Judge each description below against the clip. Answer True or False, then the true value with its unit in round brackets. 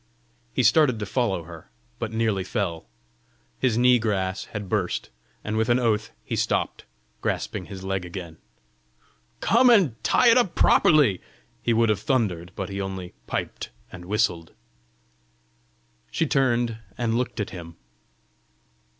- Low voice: True (110 Hz)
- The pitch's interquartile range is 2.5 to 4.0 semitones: False (4.4 semitones)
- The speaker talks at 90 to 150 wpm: True (140 wpm)